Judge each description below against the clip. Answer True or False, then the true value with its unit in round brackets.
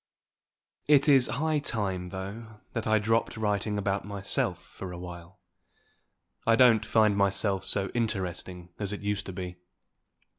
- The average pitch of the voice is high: False (100 Hz)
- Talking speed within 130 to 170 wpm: True (150 wpm)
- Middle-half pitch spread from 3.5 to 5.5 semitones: False (2.9 semitones)